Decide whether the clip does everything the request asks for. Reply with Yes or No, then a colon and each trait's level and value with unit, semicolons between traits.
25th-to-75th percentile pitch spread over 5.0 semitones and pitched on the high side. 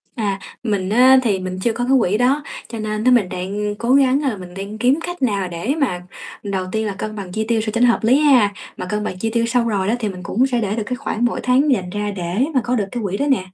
No: average, 3.8 semitones; high, 220 Hz